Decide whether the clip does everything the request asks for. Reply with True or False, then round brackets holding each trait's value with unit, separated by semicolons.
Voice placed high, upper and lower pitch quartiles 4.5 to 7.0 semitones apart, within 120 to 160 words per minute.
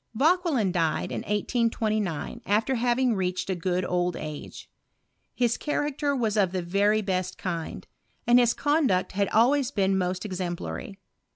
True (205 Hz; 5.0 semitones; 150 wpm)